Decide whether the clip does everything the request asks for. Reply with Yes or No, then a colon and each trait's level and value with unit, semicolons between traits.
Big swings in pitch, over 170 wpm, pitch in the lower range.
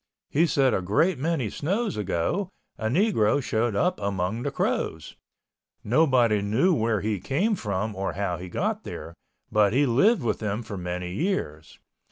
No: wide, 7.0 semitones; average, 165 wpm; low, 110 Hz